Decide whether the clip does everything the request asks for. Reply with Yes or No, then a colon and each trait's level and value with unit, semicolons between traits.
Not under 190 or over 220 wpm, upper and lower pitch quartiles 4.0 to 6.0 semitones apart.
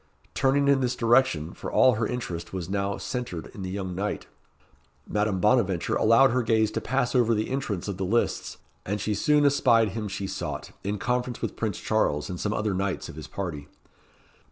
Yes: average, 195 wpm; average, 4.4 semitones